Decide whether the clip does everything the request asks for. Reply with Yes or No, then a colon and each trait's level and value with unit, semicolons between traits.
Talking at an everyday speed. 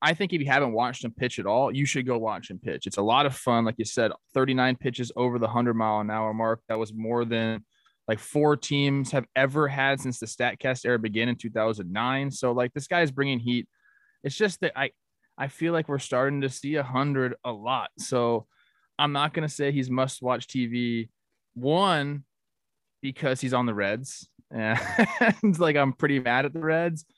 No: fast, 210 wpm